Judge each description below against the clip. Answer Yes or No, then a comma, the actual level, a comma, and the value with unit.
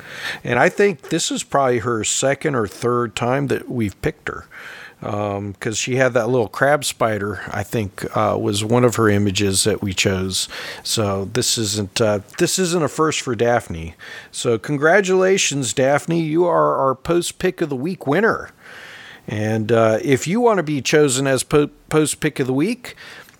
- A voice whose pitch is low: Yes, low, 125 Hz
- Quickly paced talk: No, average, 180 wpm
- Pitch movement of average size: No, wide, 6.3 semitones